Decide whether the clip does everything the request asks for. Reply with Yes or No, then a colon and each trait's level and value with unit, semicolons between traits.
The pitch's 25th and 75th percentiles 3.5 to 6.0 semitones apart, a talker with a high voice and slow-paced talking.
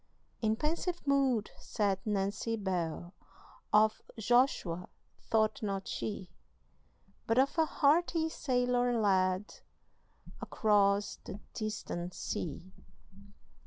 Yes: average, 4.3 semitones; high, 215 Hz; slow, 90 wpm